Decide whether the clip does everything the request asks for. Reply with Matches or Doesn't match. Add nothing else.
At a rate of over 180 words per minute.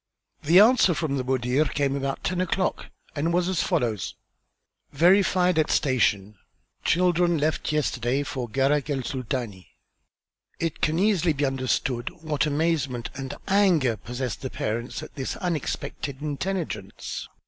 Doesn't match